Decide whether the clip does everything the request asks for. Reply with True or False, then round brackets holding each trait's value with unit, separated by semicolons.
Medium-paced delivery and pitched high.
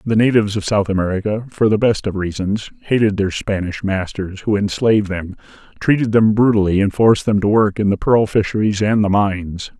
False (195 wpm; 105 Hz)